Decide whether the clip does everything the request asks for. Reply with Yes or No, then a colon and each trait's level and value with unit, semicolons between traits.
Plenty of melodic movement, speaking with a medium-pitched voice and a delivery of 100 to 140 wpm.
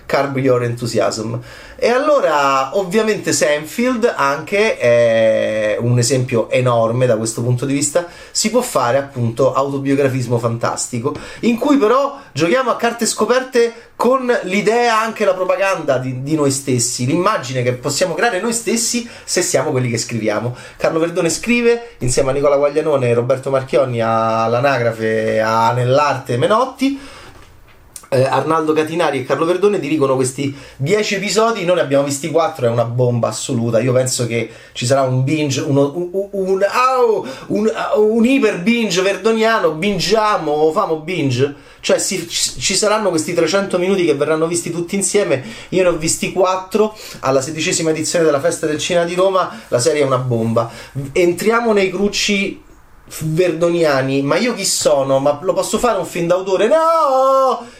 No: wide, 7.7 semitones; medium, 160 Hz; average, 155 wpm